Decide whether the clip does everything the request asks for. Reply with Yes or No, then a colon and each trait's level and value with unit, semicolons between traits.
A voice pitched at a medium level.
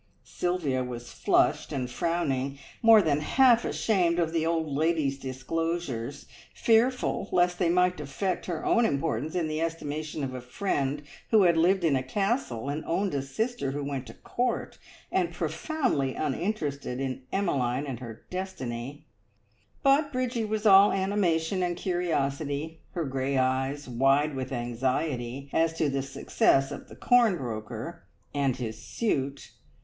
Yes: medium, 150 Hz